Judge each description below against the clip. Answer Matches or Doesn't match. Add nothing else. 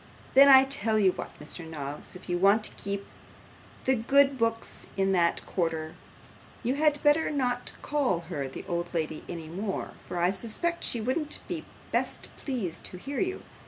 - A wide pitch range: Matches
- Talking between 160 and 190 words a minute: Matches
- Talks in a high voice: Matches